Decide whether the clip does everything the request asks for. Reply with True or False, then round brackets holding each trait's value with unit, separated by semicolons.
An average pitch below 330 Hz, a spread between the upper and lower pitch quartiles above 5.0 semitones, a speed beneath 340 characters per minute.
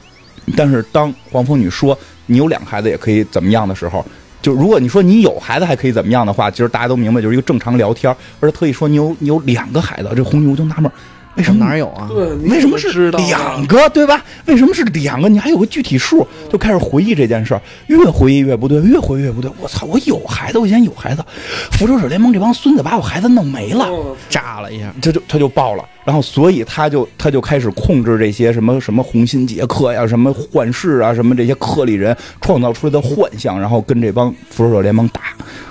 False (135 Hz; 5.5 semitones; 355 characters per minute)